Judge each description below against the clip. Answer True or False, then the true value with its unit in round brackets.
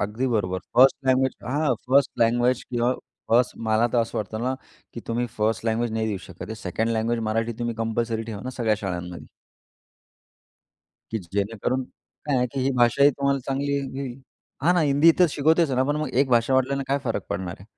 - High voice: False (120 Hz)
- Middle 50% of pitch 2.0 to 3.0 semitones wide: False (3.4 semitones)